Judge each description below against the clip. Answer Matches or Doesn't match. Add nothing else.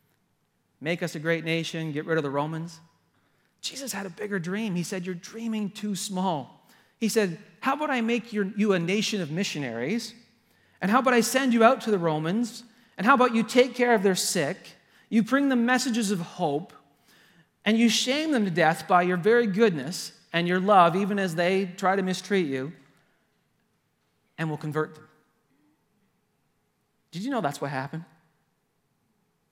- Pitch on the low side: Doesn't match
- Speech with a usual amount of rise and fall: Doesn't match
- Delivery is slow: Doesn't match